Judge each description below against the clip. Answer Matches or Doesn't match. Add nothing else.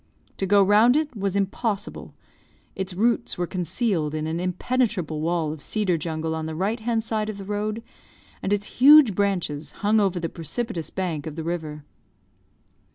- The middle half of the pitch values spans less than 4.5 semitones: Doesn't match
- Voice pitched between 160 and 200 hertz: Matches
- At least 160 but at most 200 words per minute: Matches